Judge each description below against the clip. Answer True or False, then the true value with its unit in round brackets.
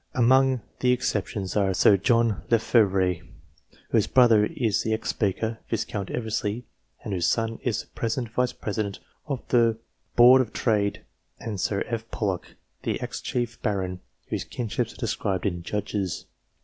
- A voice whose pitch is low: True (110 Hz)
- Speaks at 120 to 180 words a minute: True (155 wpm)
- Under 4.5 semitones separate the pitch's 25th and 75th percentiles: True (3.0 semitones)